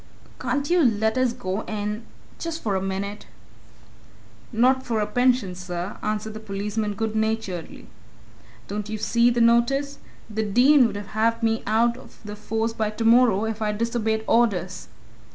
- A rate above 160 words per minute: No, average, 155 wpm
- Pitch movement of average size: No, narrow, 2.3 semitones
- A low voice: No, high, 220 Hz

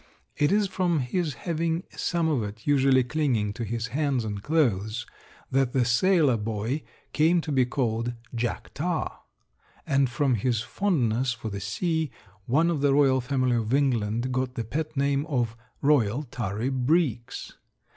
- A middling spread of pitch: Yes, average, 4.7 semitones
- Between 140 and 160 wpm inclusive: Yes, average, 155 wpm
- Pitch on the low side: Yes, low, 130 Hz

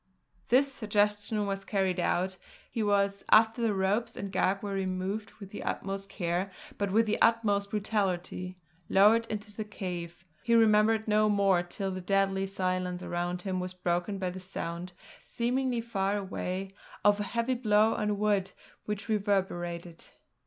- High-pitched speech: Yes, high, 200 Hz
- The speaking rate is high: No, average, 155 wpm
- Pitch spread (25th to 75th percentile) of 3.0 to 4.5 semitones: No, narrow, 2.4 semitones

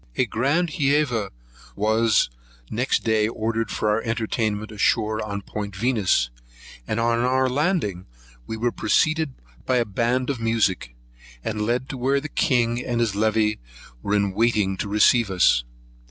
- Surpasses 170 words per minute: No, average, 155 wpm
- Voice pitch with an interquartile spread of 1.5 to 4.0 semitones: Yes, average, 3.0 semitones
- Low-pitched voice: Yes, low, 115 Hz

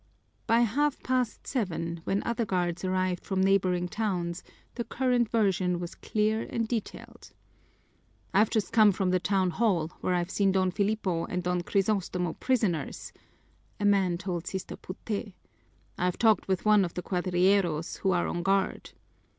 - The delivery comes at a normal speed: Yes, average, 155 wpm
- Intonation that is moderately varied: Yes, average, 3.1 semitones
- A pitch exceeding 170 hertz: Yes, high, 190 Hz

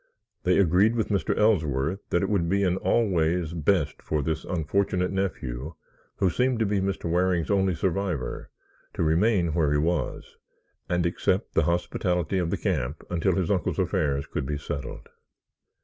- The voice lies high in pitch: No, very low, 90 Hz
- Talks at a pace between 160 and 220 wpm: Yes, average, 165 wpm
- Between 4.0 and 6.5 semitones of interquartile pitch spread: No, average, 3.6 semitones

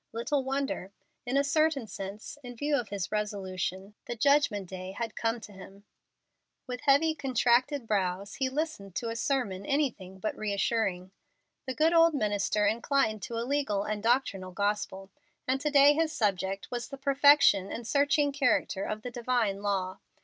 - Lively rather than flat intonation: Yes, wide, 5.7 semitones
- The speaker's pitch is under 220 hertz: No, high, 230 Hz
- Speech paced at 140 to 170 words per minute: Yes, average, 165 wpm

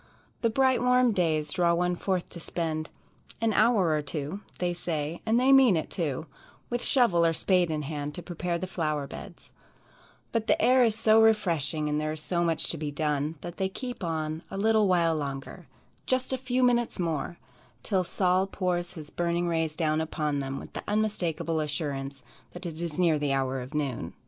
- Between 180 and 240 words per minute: Yes, average, 195 wpm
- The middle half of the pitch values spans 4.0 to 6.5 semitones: Yes, average, 4.7 semitones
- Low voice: No, medium, 170 Hz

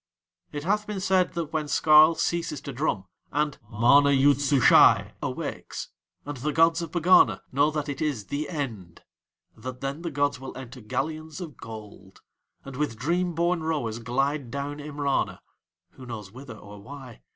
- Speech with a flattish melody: No, average, 3.8 semitones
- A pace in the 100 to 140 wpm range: No, average, 165 wpm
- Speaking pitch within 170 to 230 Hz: No, medium, 145 Hz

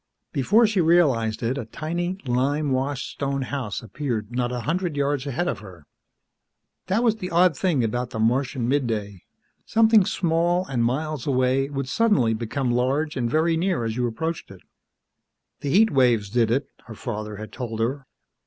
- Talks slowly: No, average, 170 wpm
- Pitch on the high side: No, low, 135 Hz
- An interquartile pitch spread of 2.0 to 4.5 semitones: No, wide, 5.5 semitones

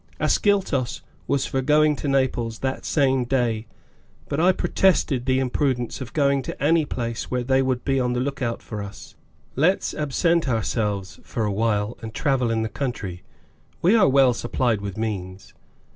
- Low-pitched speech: Yes, low, 130 Hz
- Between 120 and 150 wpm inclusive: No, average, 170 wpm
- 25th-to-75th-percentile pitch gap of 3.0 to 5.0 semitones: Yes, average, 3.6 semitones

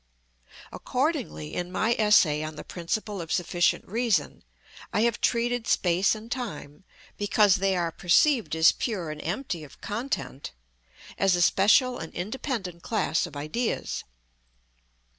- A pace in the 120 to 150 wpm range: Yes, slow, 135 wpm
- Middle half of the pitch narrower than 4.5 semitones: No, wide, 5.4 semitones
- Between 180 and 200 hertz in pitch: Yes, high, 190 Hz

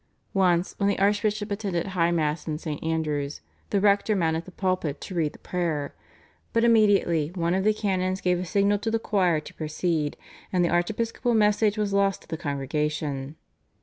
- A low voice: No, medium, 180 Hz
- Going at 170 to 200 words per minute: Yes, average, 180 wpm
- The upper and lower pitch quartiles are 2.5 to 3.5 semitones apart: No, average, 4.2 semitones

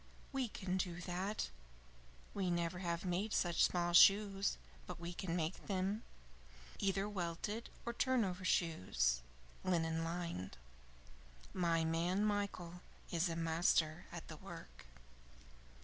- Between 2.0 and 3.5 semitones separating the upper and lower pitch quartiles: Yes, average, 2.8 semitones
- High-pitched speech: No, medium, 175 Hz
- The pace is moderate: No, slow, 120 wpm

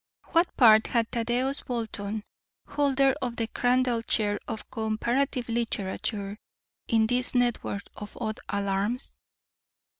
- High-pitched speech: Yes, high, 230 Hz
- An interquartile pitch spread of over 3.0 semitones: No, narrow, 2.6 semitones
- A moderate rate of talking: No, slow, 115 wpm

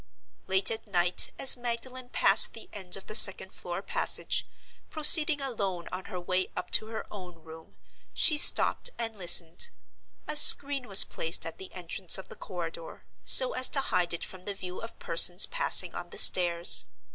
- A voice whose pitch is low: No, high, 190 Hz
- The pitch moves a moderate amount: No, wide, 5.8 semitones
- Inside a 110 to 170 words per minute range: No, average, 180 wpm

